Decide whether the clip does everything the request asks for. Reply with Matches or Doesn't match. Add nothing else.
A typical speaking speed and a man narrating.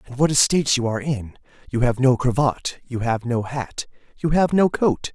Doesn't match